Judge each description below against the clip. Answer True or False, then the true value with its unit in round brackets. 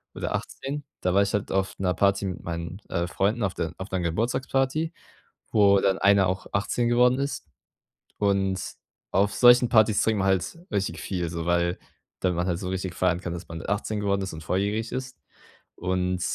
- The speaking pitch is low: True (95 Hz)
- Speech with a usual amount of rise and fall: True (3.1 semitones)